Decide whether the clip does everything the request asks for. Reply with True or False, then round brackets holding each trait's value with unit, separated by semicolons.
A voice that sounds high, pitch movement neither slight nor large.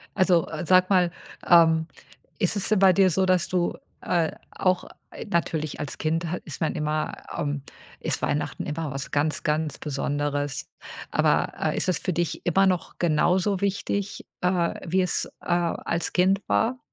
False (175 Hz; 3.1 semitones)